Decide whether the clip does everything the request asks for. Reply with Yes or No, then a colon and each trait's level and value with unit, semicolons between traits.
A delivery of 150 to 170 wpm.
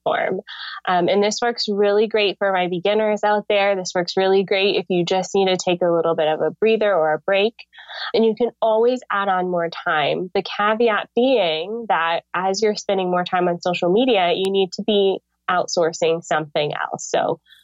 No: average, 195 wpm